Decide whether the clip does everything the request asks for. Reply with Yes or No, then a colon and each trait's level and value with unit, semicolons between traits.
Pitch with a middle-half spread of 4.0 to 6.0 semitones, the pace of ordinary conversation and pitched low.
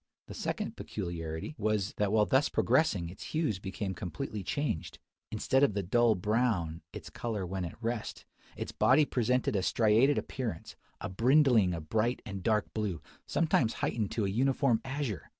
Yes: average, 4.9 semitones; average, 165 wpm; low, 110 Hz